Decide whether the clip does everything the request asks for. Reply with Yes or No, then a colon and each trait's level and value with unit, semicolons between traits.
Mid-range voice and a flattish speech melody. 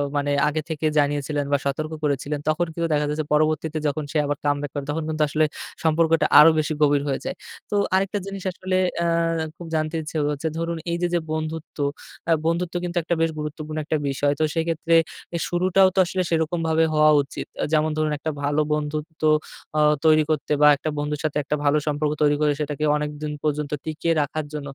Yes: medium, 155 Hz; narrow, 1.8 semitones